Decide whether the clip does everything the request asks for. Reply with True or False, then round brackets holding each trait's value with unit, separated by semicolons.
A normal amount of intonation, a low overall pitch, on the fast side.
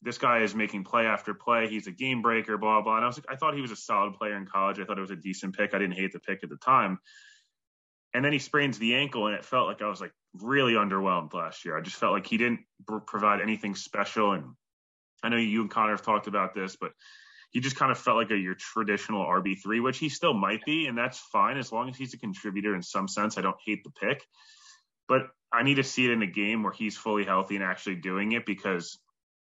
True (3.8 semitones; 110 Hz; 265 wpm)